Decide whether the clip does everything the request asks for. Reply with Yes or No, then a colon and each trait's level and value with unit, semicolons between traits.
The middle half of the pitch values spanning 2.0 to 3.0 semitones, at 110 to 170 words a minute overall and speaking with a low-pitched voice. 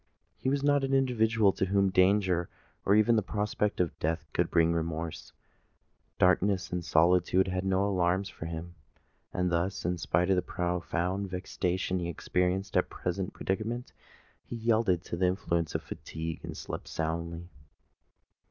Yes: average, 2.7 semitones; average, 155 wpm; very low, 90 Hz